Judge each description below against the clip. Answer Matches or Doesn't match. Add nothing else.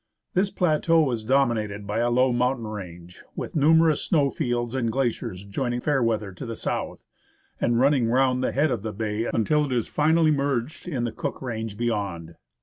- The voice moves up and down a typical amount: Matches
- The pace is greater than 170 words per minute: Matches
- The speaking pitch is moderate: Doesn't match